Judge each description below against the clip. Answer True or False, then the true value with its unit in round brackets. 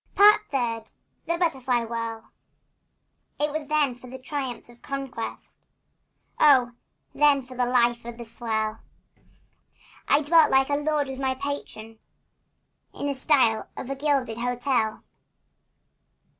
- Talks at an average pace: False (130 wpm)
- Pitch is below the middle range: False (260 Hz)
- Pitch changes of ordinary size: True (3.3 semitones)